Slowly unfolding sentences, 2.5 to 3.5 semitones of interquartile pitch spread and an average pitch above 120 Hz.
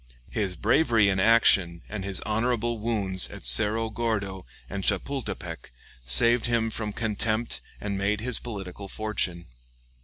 No: slow, 130 wpm; average, 3.0 semitones; low, 105 Hz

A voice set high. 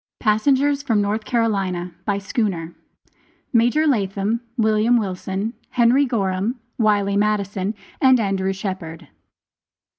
Yes: high, 210 Hz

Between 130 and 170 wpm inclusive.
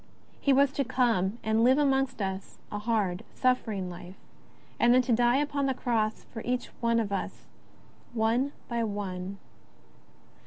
Yes: average, 150 wpm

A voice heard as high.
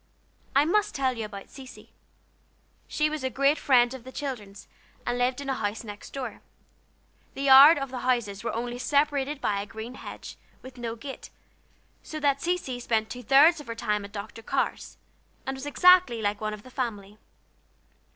Yes: very high, 255 Hz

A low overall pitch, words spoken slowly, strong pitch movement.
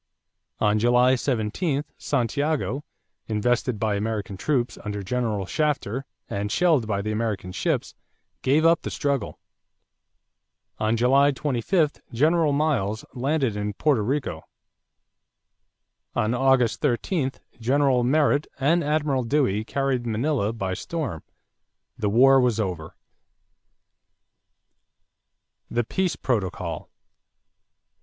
No: low, 125 Hz; slow, 105 wpm; average, 5.0 semitones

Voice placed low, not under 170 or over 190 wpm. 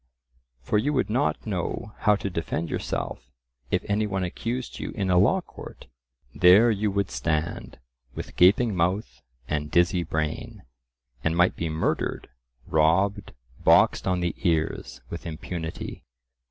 No: very low, 90 Hz; average, 140 wpm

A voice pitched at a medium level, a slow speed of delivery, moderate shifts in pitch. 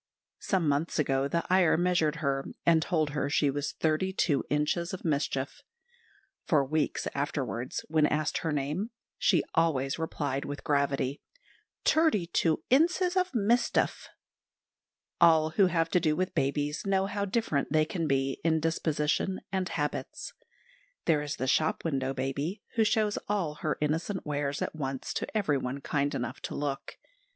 No: medium, 155 Hz; average, 155 wpm; average, 4.1 semitones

